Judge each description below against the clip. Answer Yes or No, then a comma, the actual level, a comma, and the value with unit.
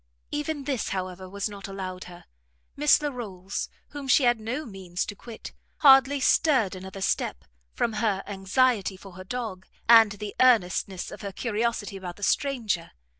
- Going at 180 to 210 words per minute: No, average, 160 wpm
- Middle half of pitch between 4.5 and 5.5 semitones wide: Yes, average, 4.8 semitones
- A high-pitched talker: Yes, high, 205 Hz